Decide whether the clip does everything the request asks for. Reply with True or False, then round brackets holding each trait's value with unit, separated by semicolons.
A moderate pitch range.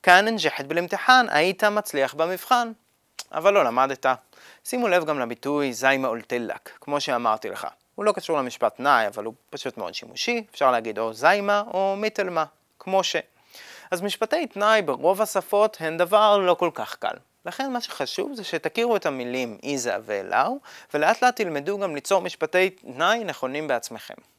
False (6.6 semitones)